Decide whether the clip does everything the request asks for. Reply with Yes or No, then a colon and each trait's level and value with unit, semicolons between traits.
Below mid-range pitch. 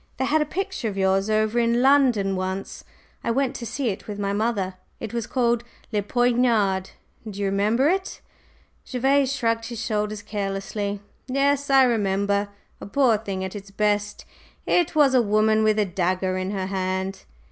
No: high, 215 Hz